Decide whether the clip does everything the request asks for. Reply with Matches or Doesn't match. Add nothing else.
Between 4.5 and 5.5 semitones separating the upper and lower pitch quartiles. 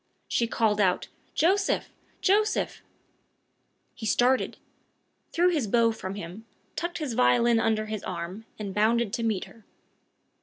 Doesn't match